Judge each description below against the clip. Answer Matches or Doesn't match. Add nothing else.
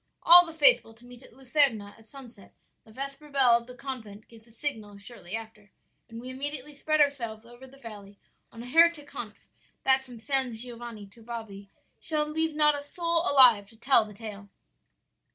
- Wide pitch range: Doesn't match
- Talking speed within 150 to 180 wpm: Doesn't match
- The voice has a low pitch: Doesn't match